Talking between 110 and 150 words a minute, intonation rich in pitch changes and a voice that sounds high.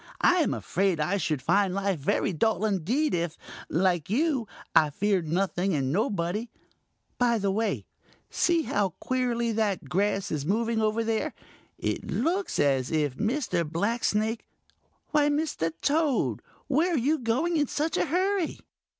Yes: average, 145 wpm; wide, 7.3 semitones; high, 215 Hz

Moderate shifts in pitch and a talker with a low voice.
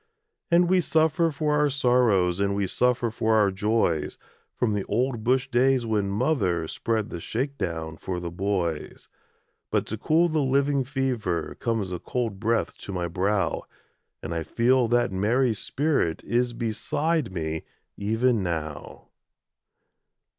No: wide, 5.8 semitones; low, 115 Hz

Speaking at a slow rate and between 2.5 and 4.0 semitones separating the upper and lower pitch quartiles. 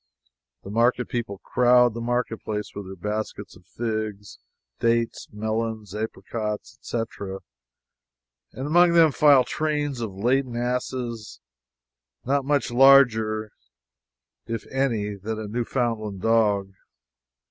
Yes: slow, 110 wpm; average, 2.8 semitones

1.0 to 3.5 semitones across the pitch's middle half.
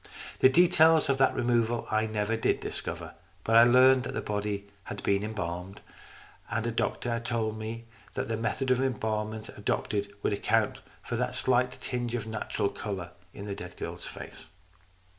Yes: average, 2.8 semitones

